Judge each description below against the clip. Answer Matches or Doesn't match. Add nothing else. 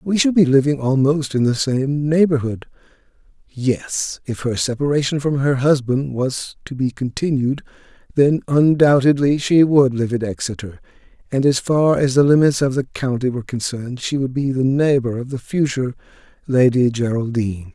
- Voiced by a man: Matches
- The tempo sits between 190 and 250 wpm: Doesn't match